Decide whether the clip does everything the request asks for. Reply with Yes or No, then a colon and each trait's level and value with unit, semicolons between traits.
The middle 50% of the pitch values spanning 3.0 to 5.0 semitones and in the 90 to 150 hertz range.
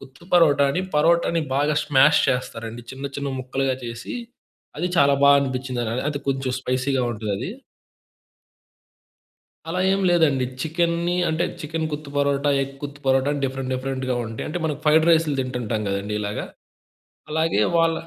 Yes: average, 3.5 semitones; medium, 140 Hz